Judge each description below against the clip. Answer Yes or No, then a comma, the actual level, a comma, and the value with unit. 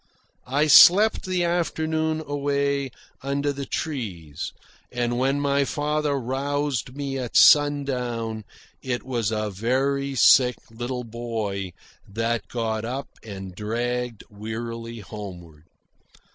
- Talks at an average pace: No, slow, 110 wpm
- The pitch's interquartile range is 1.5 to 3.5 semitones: No, average, 4.0 semitones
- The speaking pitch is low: Yes, low, 125 Hz